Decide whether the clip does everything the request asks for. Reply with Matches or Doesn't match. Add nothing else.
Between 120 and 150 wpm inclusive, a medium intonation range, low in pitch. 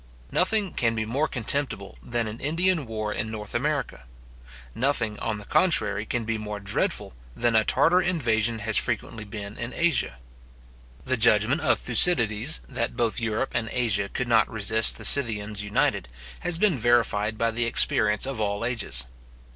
Doesn't match